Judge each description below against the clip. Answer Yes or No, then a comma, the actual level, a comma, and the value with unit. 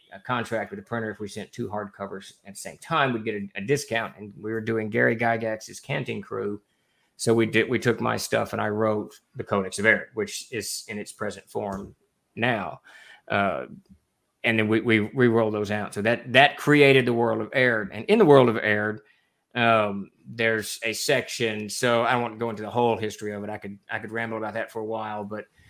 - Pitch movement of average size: No, narrow, 1.9 semitones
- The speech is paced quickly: Yes, fast, 230 wpm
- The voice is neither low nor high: No, low, 110 Hz